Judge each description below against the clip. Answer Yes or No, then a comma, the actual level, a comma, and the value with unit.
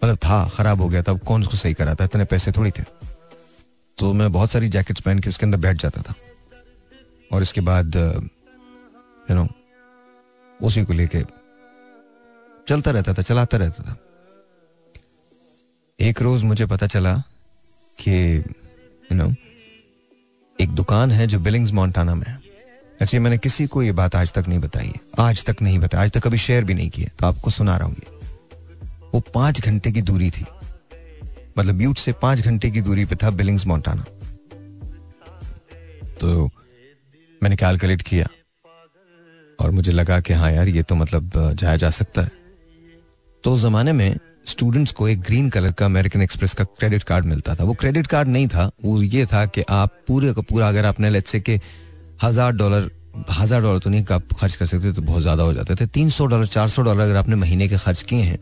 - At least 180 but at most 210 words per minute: Yes, average, 185 wpm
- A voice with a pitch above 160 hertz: No, low, 100 Hz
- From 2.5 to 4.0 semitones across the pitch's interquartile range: No, average, 5.1 semitones